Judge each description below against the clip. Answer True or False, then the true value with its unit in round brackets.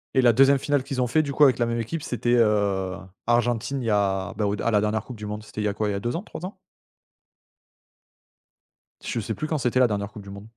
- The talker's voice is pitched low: True (115 Hz)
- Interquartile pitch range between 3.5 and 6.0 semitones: True (3.8 semitones)